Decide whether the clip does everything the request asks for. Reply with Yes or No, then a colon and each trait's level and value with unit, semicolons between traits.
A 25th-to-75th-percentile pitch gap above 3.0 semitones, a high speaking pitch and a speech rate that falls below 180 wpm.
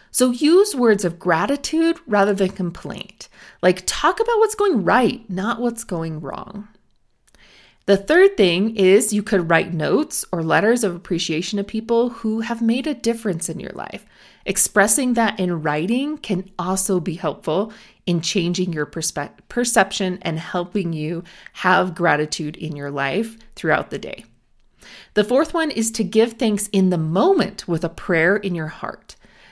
Yes: average, 4.8 semitones; high, 195 Hz; average, 165 wpm